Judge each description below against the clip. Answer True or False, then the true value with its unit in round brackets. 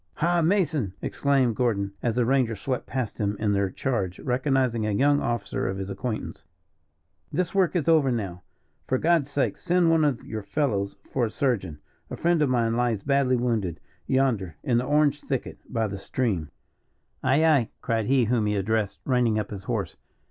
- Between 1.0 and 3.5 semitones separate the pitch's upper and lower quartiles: False (5.0 semitones)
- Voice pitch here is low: True (120 Hz)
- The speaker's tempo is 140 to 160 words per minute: False (185 wpm)